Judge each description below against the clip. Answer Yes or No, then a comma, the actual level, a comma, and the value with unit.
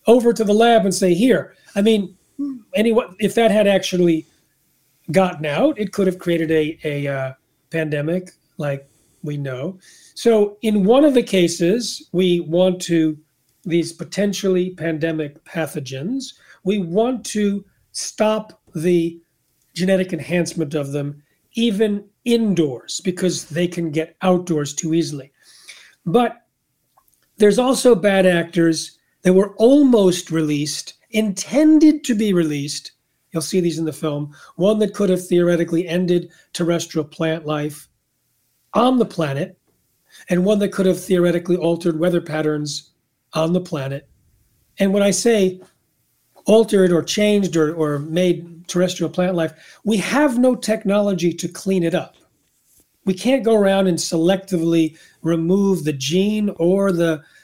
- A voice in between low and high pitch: Yes, medium, 180 Hz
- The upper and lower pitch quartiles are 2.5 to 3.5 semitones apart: No, average, 4.1 semitones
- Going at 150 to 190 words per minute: No, average, 140 wpm